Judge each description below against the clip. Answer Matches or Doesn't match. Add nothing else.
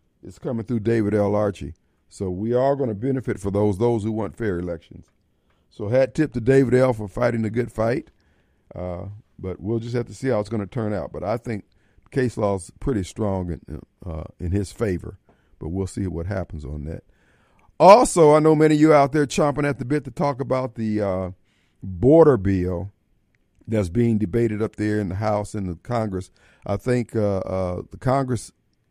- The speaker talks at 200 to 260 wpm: Matches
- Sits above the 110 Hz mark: Doesn't match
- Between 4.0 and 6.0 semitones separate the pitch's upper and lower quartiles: Matches